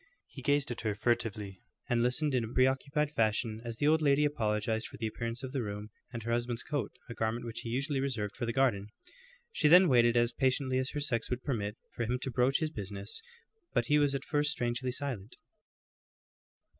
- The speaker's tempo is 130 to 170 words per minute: No, fast, 205 wpm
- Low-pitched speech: Yes, low, 120 Hz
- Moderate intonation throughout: Yes, average, 3.5 semitones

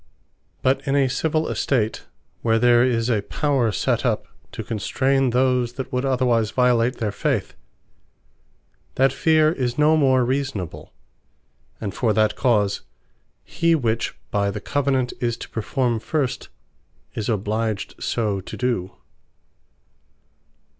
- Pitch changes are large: No, average, 3.4 semitones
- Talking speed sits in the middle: No, slow, 130 wpm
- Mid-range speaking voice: No, low, 125 Hz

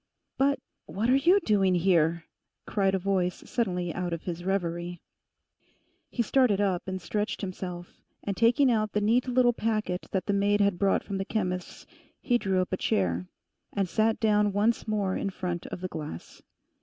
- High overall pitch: Yes, high, 195 Hz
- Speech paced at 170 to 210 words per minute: Yes, average, 180 wpm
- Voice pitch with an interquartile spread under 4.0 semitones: Yes, average, 3.2 semitones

